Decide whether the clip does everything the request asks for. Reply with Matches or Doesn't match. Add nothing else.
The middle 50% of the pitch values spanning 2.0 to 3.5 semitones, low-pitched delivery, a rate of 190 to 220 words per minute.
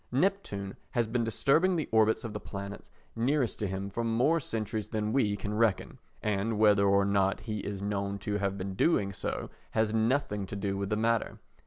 Matches